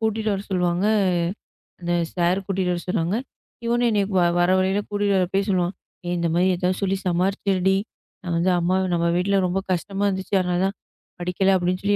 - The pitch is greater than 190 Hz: No, medium, 185 Hz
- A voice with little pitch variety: Yes, narrow, 2.0 semitones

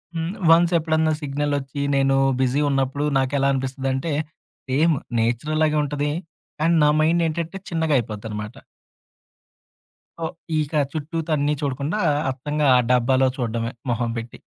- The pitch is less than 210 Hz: Yes, medium, 140 Hz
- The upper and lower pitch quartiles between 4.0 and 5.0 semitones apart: No, average, 3.3 semitones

